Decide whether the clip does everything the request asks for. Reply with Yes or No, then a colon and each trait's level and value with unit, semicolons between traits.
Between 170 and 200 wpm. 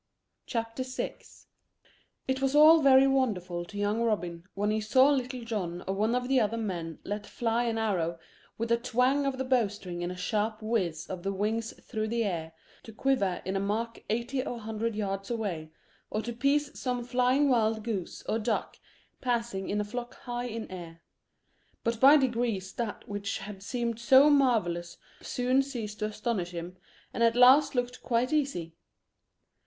Yes: average, 180 wpm